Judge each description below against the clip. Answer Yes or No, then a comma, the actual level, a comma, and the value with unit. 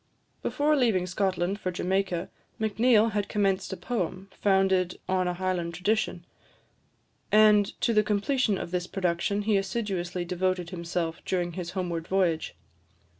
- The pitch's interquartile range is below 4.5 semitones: Yes, narrow, 2.6 semitones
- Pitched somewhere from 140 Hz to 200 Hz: Yes, high, 190 Hz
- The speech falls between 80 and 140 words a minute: Yes, slow, 135 wpm